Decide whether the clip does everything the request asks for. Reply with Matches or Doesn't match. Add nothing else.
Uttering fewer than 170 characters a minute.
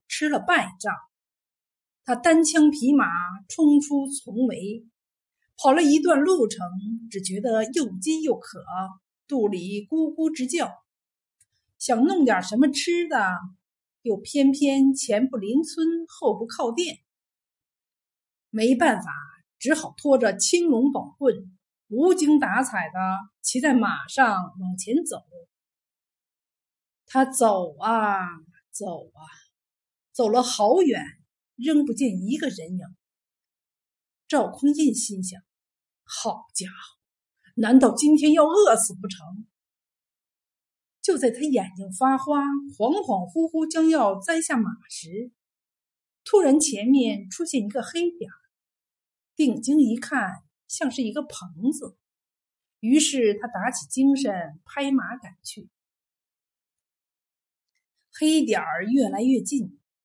Matches